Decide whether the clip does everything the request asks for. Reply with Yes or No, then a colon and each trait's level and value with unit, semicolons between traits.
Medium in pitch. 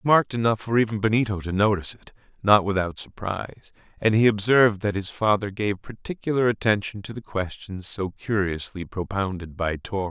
No: low, 105 Hz